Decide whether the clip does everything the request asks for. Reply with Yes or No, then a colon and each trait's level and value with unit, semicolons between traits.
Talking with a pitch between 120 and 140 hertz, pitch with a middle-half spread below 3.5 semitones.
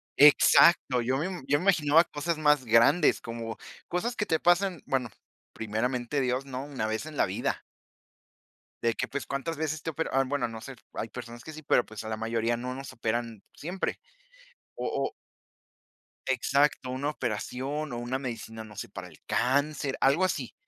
No: low, 135 Hz; average, 4.3 semitones